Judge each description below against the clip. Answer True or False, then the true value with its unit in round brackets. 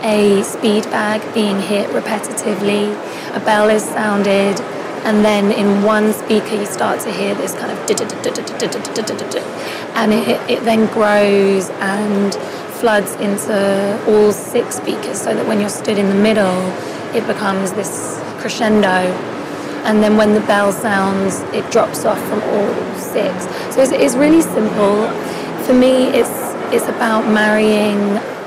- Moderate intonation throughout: False (1.3 semitones)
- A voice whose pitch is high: True (210 Hz)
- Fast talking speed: False (145 wpm)